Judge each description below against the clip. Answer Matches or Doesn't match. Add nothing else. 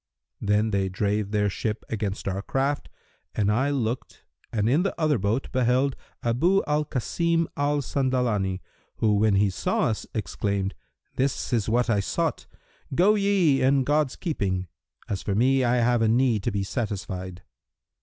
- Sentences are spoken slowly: Doesn't match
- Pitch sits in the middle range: Doesn't match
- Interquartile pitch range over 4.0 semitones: Matches